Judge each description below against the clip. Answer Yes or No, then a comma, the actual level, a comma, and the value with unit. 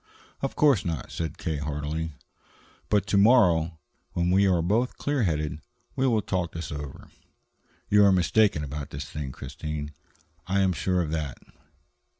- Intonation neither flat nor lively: Yes, average, 4.8 semitones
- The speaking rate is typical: Yes, average, 155 wpm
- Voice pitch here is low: Yes, very low, 85 Hz